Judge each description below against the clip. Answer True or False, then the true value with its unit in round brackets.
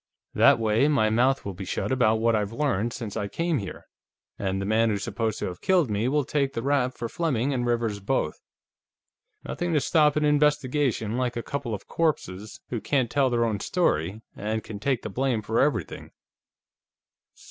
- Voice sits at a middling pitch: False (120 Hz)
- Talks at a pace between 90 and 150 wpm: False (190 wpm)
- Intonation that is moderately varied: True (4.6 semitones)